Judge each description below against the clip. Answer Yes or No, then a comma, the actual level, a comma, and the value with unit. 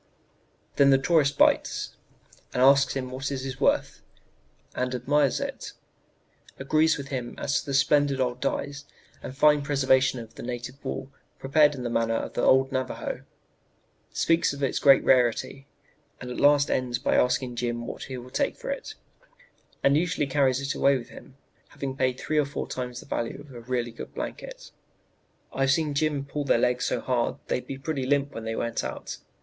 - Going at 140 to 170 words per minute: No, average, 190 wpm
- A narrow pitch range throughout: Yes, narrow, 2.3 semitones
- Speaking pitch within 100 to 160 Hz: Yes, low, 135 Hz